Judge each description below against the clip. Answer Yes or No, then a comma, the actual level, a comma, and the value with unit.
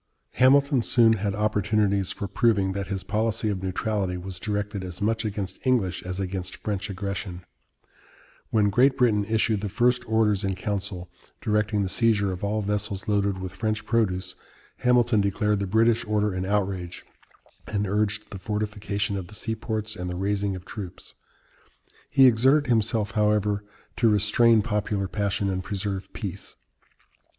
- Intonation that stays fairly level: Yes, narrow, 2.2 semitones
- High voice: No, low, 105 Hz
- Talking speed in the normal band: Yes, average, 155 wpm